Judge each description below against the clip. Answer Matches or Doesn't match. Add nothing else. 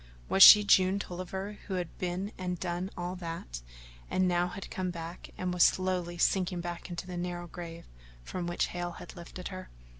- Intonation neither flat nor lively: Doesn't match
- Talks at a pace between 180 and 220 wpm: Matches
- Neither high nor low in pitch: Matches